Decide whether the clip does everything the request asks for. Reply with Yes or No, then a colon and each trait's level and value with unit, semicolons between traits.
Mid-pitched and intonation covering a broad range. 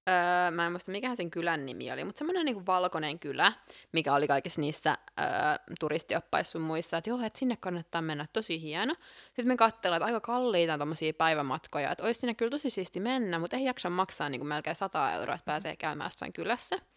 Yes: medium, 180 Hz; wide, 6.6 semitones